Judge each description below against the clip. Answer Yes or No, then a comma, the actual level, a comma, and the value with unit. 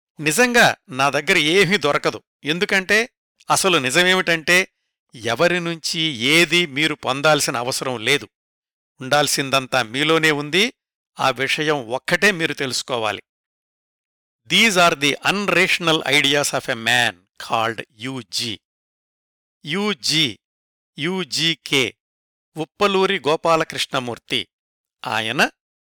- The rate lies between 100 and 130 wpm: No, average, 90 wpm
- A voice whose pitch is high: No, medium, 155 Hz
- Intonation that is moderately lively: Yes, average, 4.9 semitones